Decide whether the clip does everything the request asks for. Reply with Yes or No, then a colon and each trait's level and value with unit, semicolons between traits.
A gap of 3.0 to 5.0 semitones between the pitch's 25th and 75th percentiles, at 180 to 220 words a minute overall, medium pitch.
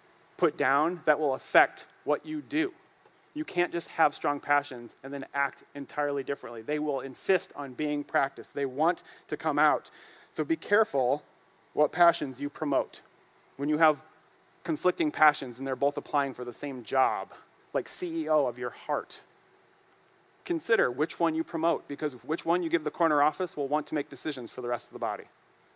Yes: average, 3.5 semitones; average, 185 wpm; medium, 150 Hz